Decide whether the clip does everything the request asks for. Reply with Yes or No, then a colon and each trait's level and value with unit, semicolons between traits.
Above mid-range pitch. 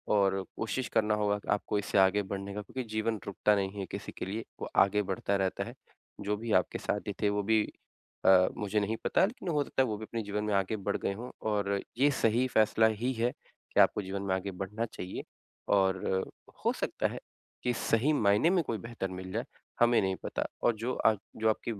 No: low, 105 Hz